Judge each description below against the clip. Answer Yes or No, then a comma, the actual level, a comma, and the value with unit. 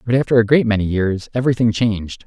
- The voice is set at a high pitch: No, low, 110 Hz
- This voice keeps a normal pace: No, fast, 210 wpm